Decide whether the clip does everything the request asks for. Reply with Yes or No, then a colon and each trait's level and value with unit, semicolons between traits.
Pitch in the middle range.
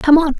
No: very high, 300 Hz